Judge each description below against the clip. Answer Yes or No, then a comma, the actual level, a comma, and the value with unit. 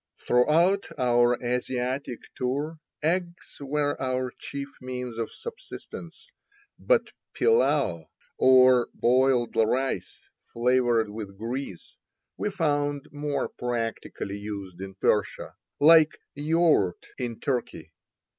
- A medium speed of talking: No, slow, 100 wpm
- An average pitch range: Yes, average, 3.8 semitones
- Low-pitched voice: Yes, low, 130 Hz